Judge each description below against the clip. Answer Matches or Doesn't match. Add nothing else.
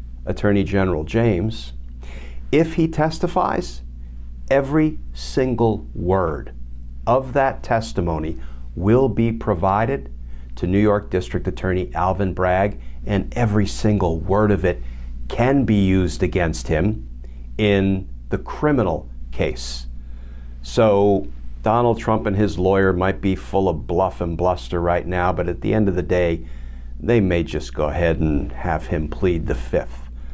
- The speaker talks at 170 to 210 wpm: Doesn't match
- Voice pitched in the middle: Doesn't match